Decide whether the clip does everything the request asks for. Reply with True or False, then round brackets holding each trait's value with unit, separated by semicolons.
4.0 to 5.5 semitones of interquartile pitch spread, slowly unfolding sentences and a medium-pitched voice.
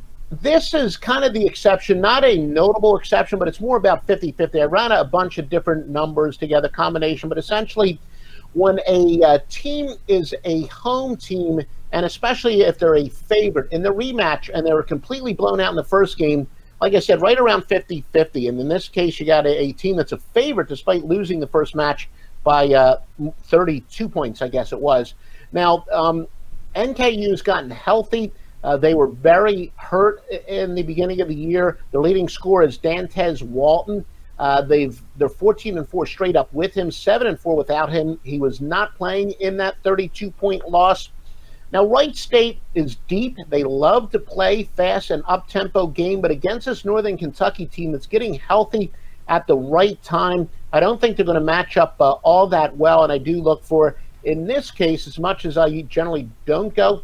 False (4.3 semitones; 195 wpm; 175 Hz)